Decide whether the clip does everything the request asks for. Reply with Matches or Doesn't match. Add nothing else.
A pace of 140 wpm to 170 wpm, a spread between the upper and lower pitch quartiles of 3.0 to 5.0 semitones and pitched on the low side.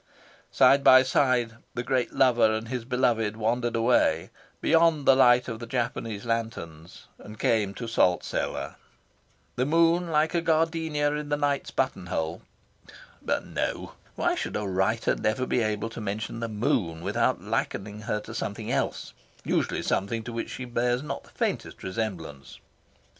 Matches